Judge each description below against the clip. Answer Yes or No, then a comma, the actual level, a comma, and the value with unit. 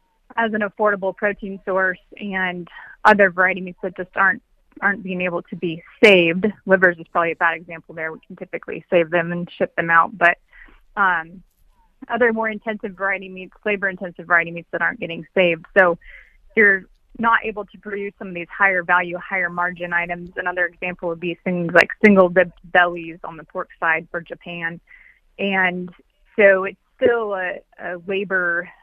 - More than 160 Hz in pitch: Yes, medium, 185 Hz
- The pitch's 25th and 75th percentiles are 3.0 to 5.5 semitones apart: No, narrow, 2.5 semitones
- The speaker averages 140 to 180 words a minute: Yes, average, 175 wpm